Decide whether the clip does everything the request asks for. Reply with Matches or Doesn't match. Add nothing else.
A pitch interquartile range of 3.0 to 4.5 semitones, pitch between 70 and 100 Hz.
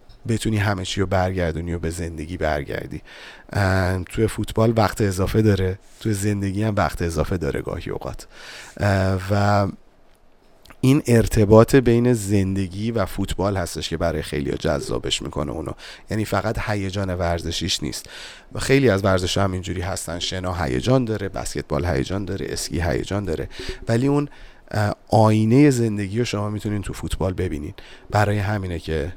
Matches